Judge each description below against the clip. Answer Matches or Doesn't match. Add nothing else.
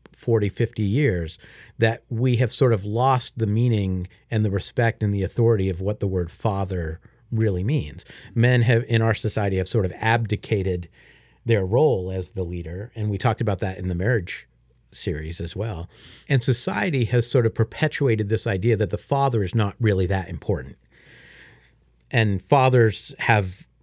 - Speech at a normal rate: Matches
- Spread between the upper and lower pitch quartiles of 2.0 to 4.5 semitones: Matches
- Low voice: Matches